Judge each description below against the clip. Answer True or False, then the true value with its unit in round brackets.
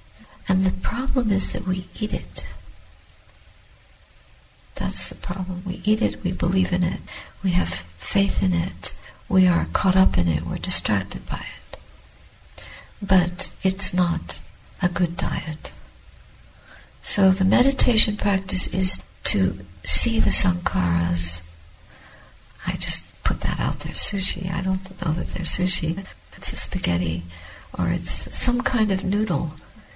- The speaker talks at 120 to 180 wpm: True (140 wpm)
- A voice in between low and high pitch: True (150 Hz)